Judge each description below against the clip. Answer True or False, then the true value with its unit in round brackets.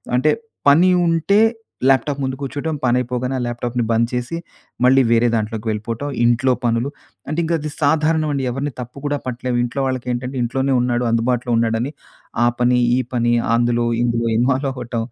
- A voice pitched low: True (125 Hz)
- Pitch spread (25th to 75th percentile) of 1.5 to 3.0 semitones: True (2.7 semitones)